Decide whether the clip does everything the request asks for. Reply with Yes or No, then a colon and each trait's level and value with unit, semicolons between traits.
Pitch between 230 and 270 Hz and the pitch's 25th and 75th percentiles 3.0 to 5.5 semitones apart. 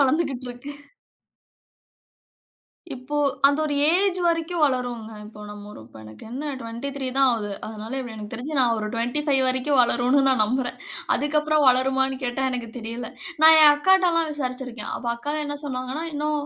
Yes: very high, 260 Hz; average, 3.6 semitones